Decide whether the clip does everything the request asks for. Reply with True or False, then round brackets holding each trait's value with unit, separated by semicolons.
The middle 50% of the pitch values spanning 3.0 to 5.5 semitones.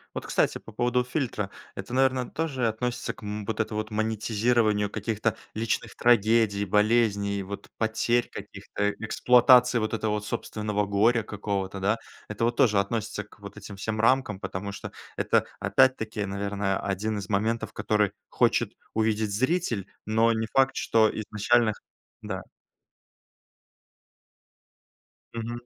False (2.4 semitones)